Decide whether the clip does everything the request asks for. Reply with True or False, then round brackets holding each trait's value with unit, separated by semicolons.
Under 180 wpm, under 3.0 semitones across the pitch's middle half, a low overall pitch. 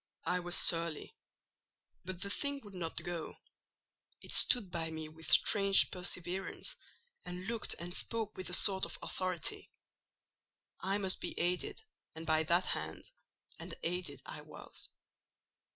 False (140 wpm; 2.5 semitones; 180 Hz)